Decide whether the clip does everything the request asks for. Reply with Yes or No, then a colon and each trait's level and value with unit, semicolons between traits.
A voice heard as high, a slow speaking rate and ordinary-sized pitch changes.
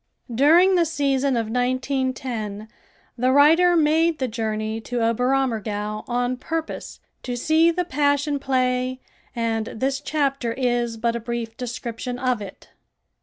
Yes: very high, 255 Hz; slow, 130 wpm; average, 3.7 semitones